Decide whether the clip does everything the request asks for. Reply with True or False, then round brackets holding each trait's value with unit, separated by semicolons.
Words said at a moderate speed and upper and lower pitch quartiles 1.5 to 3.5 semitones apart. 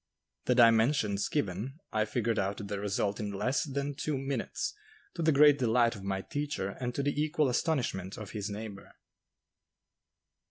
False (160 wpm; 5.5 semitones)